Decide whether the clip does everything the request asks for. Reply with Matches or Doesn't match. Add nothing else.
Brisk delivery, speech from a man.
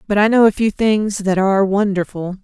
Doesn't match